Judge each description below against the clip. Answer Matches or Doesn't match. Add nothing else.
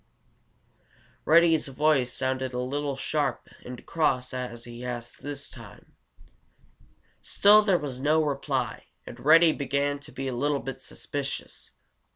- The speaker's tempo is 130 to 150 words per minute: Matches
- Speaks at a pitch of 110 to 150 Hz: Matches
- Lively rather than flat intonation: Doesn't match